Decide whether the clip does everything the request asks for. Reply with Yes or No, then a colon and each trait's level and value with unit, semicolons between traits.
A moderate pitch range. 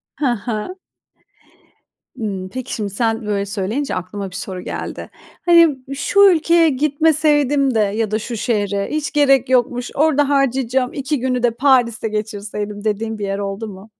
Yes: average, 5.0 semitones